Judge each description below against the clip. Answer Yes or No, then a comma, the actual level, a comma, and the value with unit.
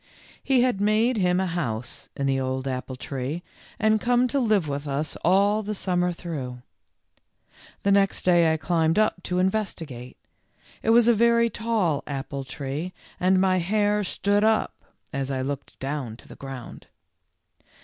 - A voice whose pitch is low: No, medium, 180 Hz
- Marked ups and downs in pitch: Yes, wide, 7.3 semitones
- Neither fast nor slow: Yes, average, 160 wpm